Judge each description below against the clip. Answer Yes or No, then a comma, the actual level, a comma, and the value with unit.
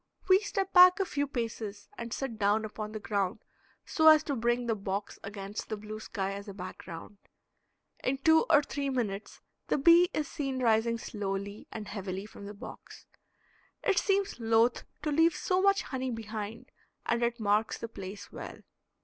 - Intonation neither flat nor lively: No, wide, 5.7 semitones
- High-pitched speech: Yes, high, 225 Hz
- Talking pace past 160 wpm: Yes, average, 175 wpm